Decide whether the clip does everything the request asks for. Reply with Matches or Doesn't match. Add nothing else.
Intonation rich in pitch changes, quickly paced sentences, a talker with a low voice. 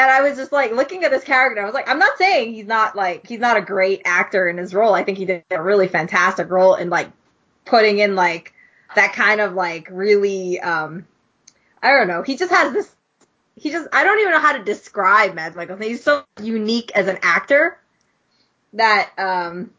Doesn't match